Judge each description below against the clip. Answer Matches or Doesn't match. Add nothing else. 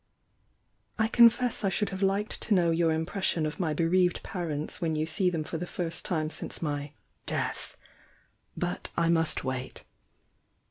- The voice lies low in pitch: Doesn't match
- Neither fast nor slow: Matches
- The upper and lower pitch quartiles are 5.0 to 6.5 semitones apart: Doesn't match